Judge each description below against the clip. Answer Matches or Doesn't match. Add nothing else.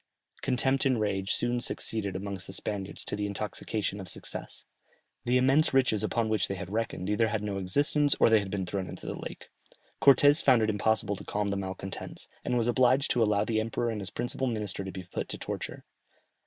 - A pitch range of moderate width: Matches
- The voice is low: Matches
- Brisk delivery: Matches